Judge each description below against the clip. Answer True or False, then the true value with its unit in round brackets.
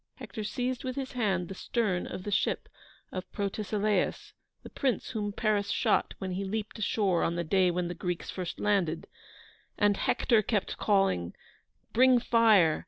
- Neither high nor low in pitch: False (205 Hz)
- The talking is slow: False (165 wpm)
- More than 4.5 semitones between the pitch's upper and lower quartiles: False (3.2 semitones)